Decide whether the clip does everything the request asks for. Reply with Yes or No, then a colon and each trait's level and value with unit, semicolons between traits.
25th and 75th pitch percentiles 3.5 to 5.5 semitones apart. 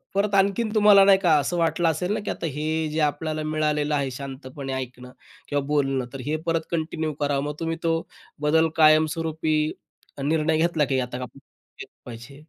No: average, 2.7 semitones